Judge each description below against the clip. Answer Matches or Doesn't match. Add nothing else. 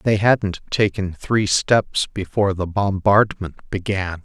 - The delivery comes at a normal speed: Doesn't match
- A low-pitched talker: Matches